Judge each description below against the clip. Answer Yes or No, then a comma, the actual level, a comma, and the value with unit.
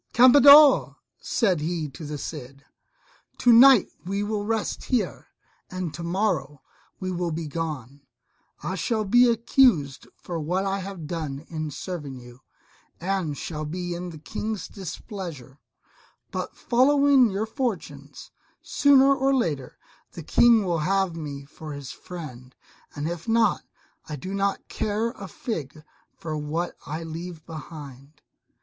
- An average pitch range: No, wide, 6.0 semitones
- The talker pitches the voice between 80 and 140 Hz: No, medium, 175 Hz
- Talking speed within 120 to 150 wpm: Yes, average, 140 wpm